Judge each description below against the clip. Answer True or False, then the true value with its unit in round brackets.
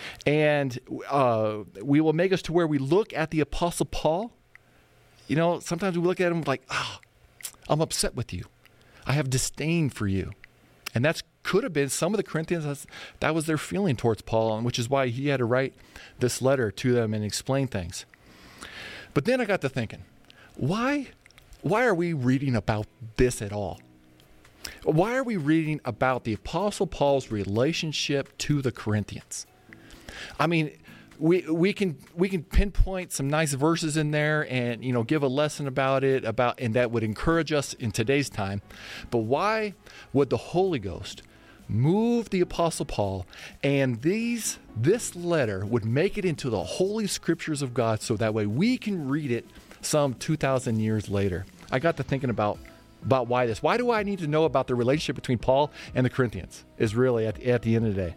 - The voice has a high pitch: False (135 Hz)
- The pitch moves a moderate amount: False (6.2 semitones)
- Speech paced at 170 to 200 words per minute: True (190 wpm)